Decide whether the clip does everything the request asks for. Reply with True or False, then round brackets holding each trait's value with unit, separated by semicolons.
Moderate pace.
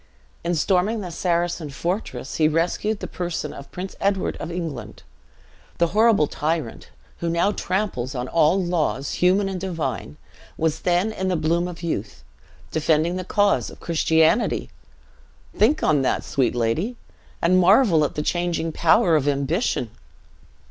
True (150 wpm)